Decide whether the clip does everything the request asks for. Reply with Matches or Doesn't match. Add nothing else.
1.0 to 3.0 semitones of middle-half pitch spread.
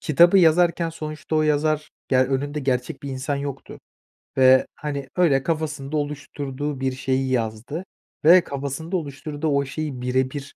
Matches